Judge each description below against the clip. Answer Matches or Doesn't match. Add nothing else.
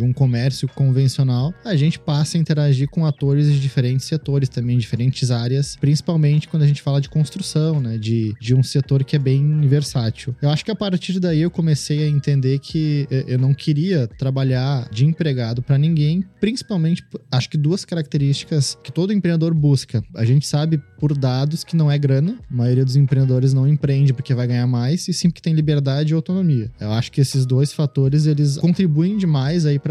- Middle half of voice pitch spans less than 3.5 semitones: Matches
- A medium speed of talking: Doesn't match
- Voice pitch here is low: Doesn't match